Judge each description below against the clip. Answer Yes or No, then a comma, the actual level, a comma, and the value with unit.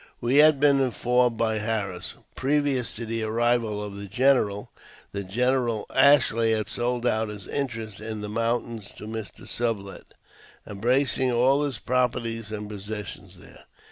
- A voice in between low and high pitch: No, low, 115 Hz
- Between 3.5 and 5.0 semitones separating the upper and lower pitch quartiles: No, average, 2.9 semitones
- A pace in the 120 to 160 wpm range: Yes, average, 145 wpm